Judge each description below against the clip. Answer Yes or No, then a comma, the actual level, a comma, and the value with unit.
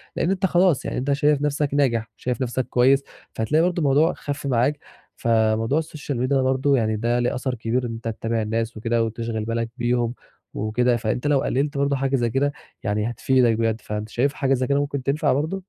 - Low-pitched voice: Yes, low, 125 Hz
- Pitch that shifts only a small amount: No, average, 3.6 semitones